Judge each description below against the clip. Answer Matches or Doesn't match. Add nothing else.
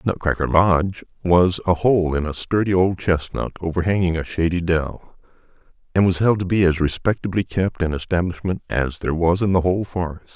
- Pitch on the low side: Matches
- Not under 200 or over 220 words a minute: Doesn't match